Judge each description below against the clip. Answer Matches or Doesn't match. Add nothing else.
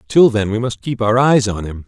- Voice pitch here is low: Matches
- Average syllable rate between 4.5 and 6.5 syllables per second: Matches